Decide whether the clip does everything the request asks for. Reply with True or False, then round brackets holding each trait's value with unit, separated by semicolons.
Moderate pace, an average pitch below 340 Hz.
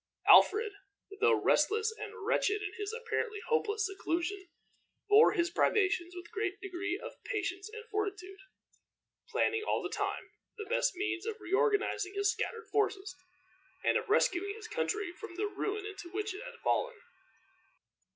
False (150 wpm; 410 Hz)